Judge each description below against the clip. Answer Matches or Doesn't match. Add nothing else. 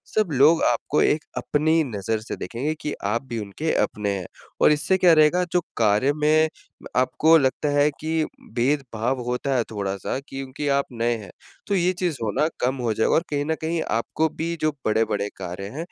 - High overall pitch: Doesn't match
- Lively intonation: Matches